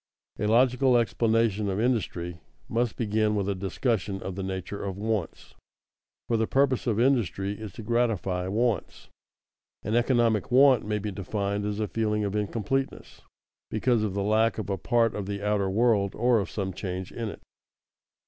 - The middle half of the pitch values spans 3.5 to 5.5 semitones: No, average, 2.9 semitones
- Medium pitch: No, low, 105 Hz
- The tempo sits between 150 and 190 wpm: Yes, average, 170 wpm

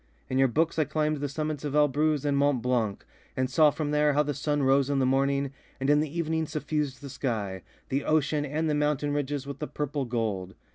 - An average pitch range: No, narrow, 2.1 semitones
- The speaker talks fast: Yes, fast, 225 wpm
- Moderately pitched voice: Yes, medium, 145 Hz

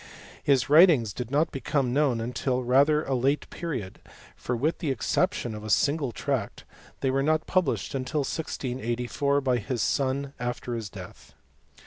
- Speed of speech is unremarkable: Yes, average, 150 wpm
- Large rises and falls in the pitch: No, average, 3.1 semitones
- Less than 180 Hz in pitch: Yes, low, 135 Hz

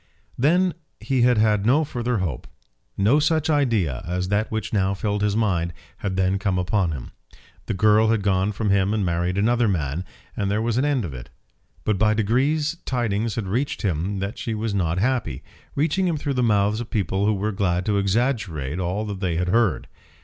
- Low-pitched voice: Yes, low, 105 Hz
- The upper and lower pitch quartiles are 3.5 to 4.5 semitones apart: Yes, average, 4.0 semitones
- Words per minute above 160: Yes, average, 200 wpm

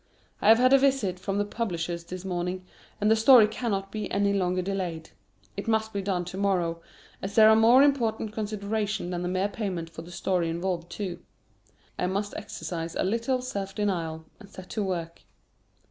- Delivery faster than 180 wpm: Yes, average, 190 wpm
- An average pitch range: Yes, average, 3.5 semitones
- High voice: Yes, high, 195 Hz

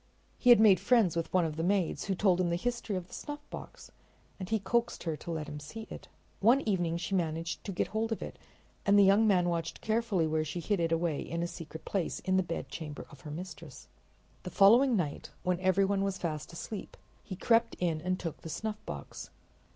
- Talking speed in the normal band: No, fast, 215 wpm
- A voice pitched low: No, medium, 185 Hz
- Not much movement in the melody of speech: No, average, 3.9 semitones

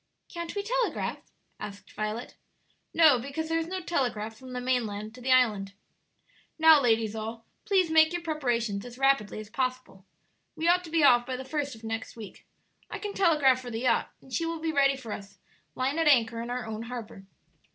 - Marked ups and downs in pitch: Yes, wide, 6.0 semitones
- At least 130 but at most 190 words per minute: No, average, 200 wpm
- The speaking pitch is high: Yes, very high, 255 Hz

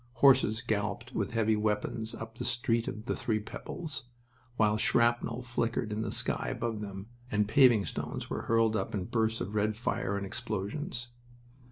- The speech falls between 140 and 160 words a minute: No, average, 170 wpm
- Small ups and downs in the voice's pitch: Yes, narrow, 2.0 semitones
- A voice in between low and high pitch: No, low, 110 Hz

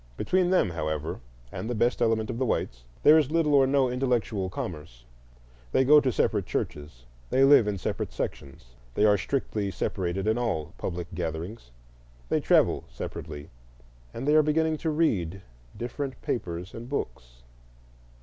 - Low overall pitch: Yes, low, 110 Hz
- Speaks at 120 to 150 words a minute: No, average, 160 wpm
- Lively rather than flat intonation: Yes, wide, 8.1 semitones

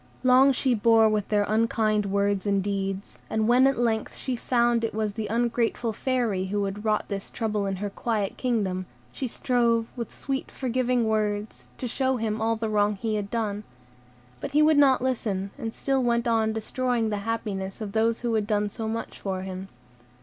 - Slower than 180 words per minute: No, average, 195 wpm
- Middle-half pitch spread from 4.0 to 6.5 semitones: No, average, 2.7 semitones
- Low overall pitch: No, high, 220 Hz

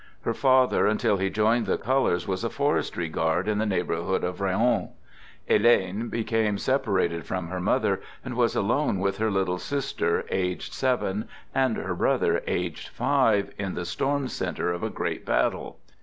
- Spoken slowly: No, average, 170 wpm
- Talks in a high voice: No, low, 100 Hz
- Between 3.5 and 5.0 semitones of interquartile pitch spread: Yes, average, 4.5 semitones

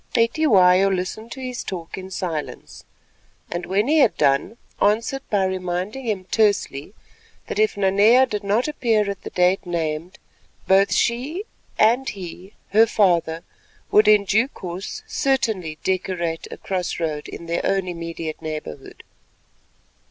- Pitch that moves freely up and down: No, average, 4.2 semitones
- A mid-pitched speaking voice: No, high, 195 Hz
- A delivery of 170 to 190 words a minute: No, average, 140 wpm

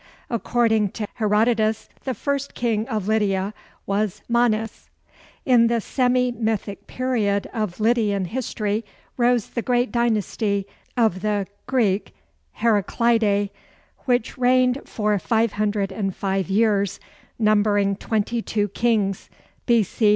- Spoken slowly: Yes, slow, 105 wpm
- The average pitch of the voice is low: No, high, 220 Hz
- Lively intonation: No, average, 2.7 semitones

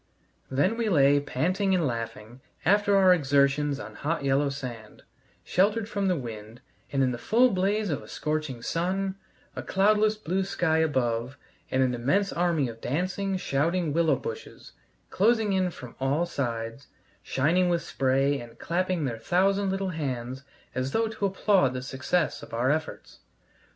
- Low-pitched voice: No, medium, 155 Hz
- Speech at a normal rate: Yes, average, 160 wpm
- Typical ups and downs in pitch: No, wide, 6.4 semitones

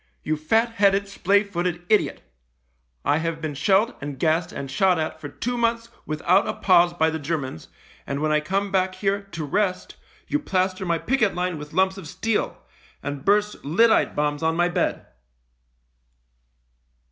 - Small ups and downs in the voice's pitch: No, average, 4.2 semitones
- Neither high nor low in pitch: Yes, medium, 180 Hz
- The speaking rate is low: No, average, 170 wpm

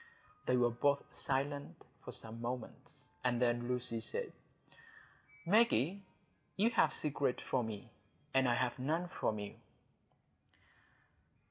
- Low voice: Yes, low, 125 Hz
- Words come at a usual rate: No, slow, 120 wpm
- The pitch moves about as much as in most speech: Yes, average, 3.2 semitones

